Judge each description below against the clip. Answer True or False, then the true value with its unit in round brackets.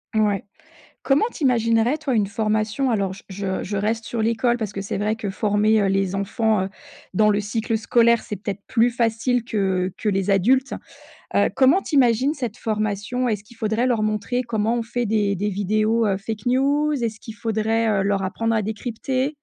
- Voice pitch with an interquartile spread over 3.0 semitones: False (2.7 semitones)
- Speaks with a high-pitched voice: True (220 Hz)